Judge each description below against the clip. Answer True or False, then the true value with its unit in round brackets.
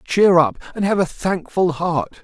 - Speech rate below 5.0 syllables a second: True (4.4 syllables/s)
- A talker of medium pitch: True (175 Hz)